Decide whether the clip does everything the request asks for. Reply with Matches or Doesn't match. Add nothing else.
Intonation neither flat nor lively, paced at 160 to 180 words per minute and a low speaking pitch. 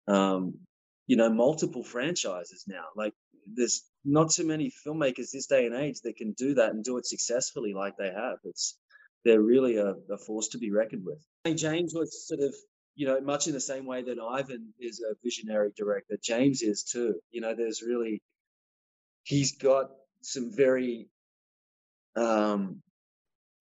Matches